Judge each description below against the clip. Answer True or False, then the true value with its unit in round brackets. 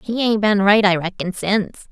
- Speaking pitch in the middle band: False (205 Hz)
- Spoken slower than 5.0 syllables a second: False (5.1 syllables/s)